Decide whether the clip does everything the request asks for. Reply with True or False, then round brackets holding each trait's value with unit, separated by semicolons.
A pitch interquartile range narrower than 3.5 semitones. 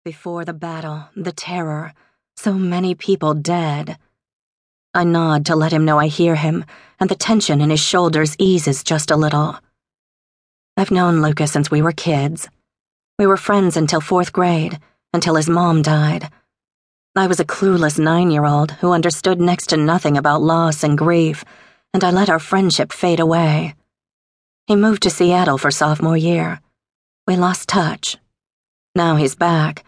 True (2.7 semitones)